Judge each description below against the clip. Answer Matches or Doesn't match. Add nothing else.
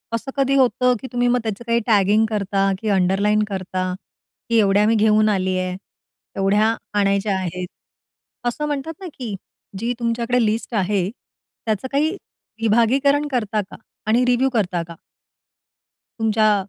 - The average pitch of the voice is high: Matches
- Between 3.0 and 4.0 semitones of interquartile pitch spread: Matches